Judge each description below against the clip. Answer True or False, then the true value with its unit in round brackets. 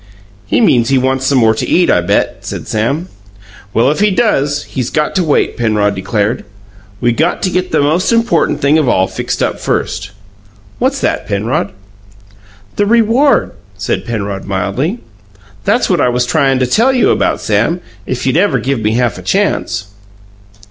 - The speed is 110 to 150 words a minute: False (175 wpm)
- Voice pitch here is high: False (130 Hz)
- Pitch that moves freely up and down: True (8.0 semitones)